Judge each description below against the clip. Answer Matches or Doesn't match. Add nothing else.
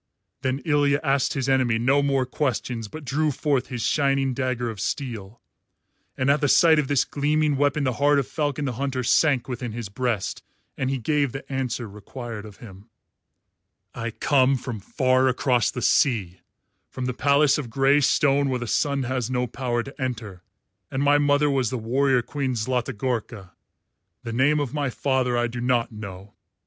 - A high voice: Doesn't match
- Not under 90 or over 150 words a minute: Doesn't match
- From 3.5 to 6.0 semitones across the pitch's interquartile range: Doesn't match